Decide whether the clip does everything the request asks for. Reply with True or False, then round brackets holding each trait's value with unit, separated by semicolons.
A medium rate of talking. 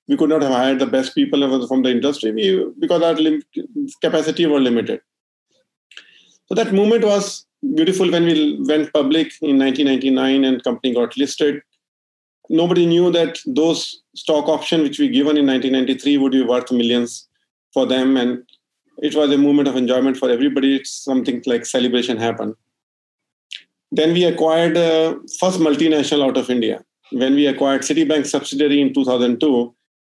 True (160 wpm)